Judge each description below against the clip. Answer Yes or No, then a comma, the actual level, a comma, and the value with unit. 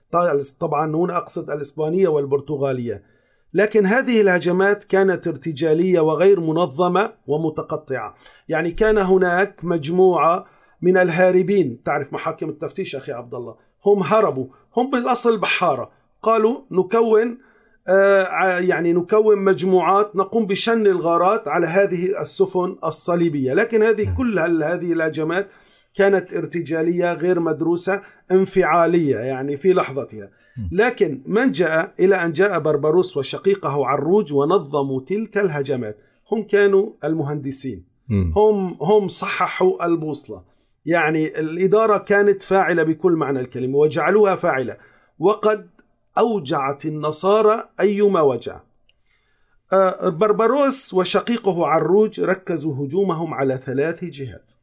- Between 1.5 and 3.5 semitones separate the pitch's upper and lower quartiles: No, average, 4.3 semitones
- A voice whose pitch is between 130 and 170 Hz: No, medium, 180 Hz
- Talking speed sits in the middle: Yes, average, 105 wpm